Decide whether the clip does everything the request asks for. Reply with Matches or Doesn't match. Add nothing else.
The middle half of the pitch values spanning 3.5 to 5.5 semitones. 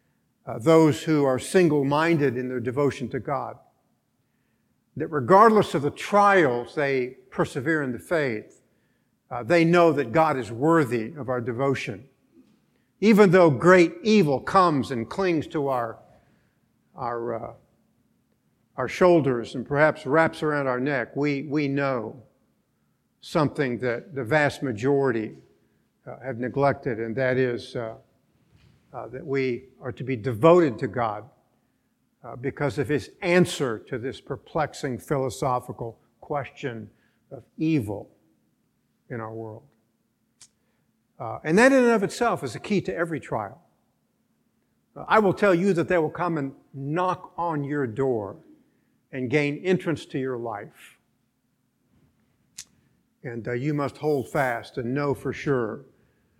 Matches